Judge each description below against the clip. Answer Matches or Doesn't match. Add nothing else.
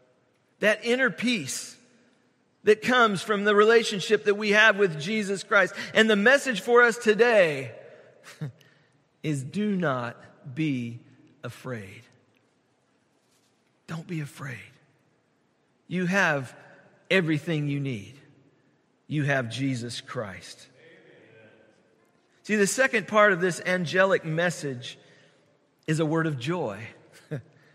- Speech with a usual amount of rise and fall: Doesn't match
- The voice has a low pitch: Doesn't match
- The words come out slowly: Matches